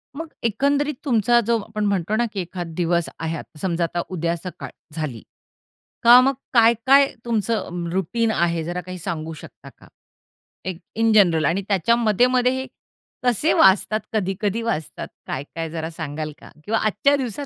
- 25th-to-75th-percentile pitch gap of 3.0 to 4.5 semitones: No, wide, 5.6 semitones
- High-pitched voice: Yes, high, 200 Hz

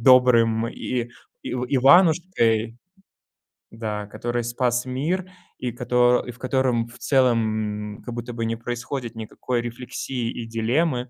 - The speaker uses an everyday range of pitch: No, narrow, 1.9 semitones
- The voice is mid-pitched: No, low, 120 Hz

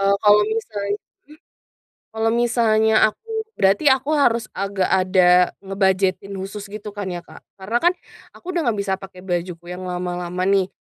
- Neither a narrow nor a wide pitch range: Yes, average, 3.0 semitones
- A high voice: Yes, high, 195 Hz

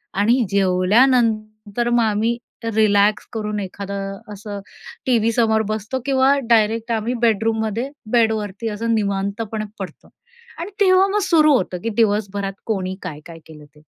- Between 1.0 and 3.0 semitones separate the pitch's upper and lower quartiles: Yes, average, 2.7 semitones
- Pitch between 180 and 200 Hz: No, high, 215 Hz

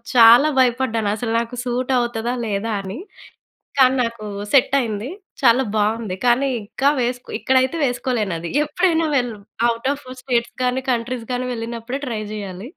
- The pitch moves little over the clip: Yes, narrow, 2.2 semitones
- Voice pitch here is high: Yes, high, 240 Hz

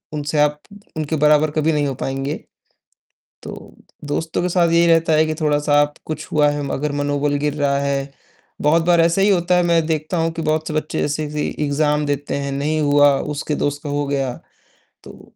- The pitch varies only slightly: Yes, narrow, 1.6 semitones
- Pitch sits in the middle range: Yes, medium, 150 Hz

